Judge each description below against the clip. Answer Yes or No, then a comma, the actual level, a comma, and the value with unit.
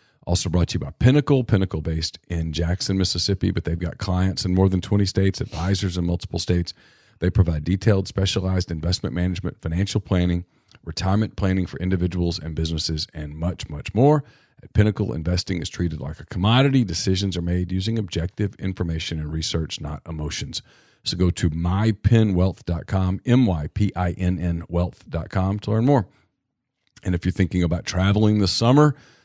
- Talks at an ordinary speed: Yes, average, 155 wpm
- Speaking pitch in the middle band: No, very low, 90 Hz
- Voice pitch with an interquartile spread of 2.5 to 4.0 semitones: Yes, average, 2.9 semitones